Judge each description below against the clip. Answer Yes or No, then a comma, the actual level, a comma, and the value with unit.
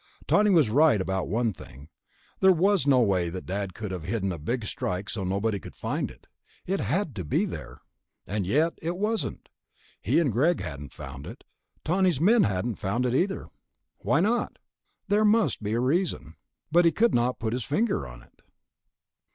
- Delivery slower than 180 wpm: No, average, 185 wpm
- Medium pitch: No, low, 120 Hz